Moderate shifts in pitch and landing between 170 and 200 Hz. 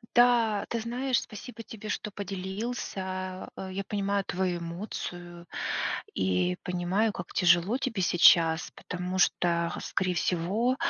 Yes: average, 3.6 semitones; high, 190 Hz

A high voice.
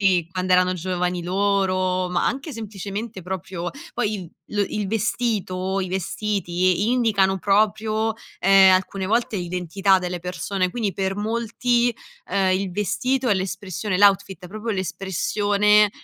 Yes: high, 195 Hz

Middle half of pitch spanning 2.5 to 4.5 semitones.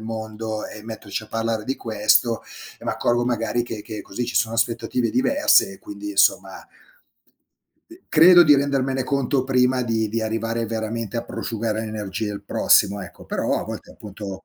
Yes: average, 2.9 semitones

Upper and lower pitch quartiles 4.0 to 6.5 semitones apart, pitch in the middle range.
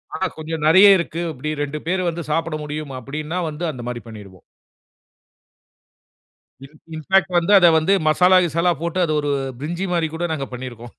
No: average, 3.2 semitones; medium, 155 Hz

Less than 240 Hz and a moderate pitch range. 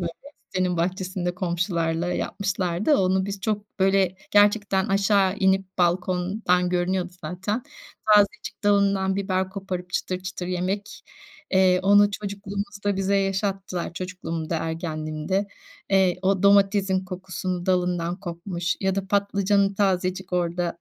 No: high, 190 Hz; narrow, 1.8 semitones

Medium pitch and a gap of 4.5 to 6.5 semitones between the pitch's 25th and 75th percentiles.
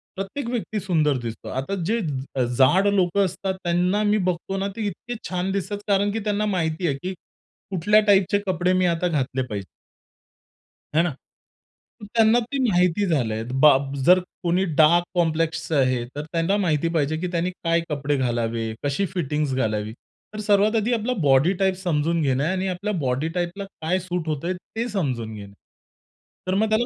Yes: medium, 175 Hz; average, 5.3 semitones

